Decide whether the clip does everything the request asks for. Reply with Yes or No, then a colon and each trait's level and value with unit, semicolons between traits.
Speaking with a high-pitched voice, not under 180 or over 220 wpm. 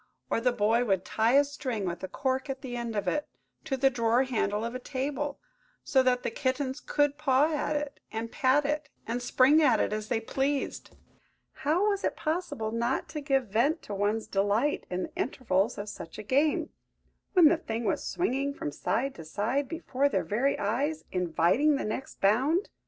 Yes: very high, 260 Hz; average, 190 wpm